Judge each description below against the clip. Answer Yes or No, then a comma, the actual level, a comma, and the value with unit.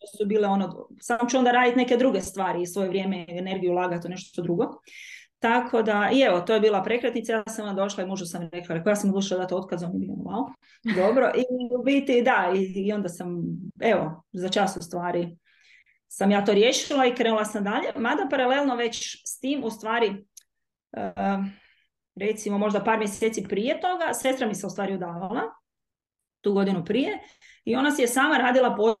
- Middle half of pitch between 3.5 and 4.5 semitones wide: Yes, average, 4.2 semitones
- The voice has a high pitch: Yes, high, 210 Hz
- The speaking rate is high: Yes, fast, 190 wpm